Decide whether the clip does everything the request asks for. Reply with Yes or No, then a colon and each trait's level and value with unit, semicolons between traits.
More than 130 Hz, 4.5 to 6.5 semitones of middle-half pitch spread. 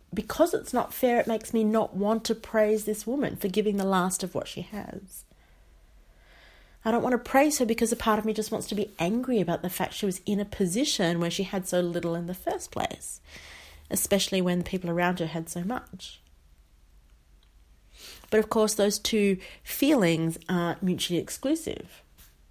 Yes: high, 190 Hz; average, 4.8 semitones